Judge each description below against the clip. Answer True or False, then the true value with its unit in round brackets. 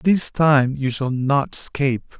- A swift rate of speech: False (165 wpm)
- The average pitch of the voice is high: False (140 Hz)